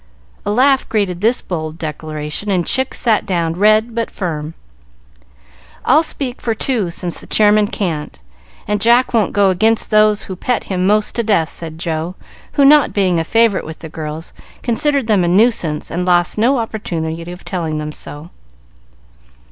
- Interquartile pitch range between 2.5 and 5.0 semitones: No, wide, 5.4 semitones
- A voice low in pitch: No, high, 195 Hz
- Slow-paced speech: No, average, 170 wpm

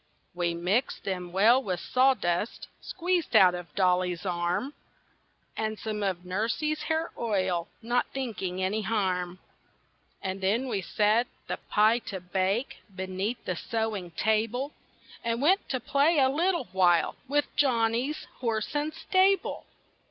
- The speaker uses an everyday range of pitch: No, wide, 5.9 semitones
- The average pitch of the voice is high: Yes, high, 215 Hz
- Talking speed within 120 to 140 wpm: Yes, slow, 135 wpm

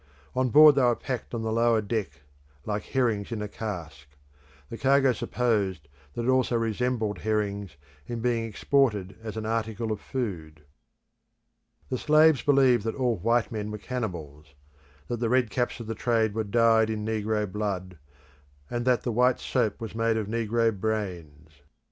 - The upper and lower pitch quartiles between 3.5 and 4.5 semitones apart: No, average, 2.8 semitones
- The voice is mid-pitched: No, low, 110 Hz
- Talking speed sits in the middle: Yes, average, 165 wpm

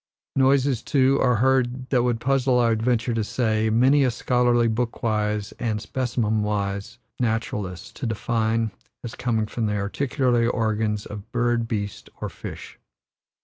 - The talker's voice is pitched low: Yes, low, 115 Hz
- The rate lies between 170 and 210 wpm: No, average, 145 wpm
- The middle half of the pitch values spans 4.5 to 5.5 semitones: No, narrow, 2.5 semitones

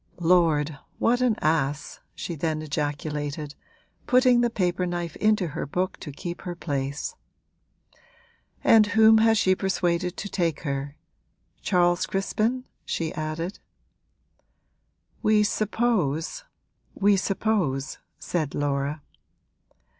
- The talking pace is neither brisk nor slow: No, slow, 110 wpm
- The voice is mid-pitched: Yes, medium, 175 Hz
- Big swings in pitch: Yes, wide, 5.7 semitones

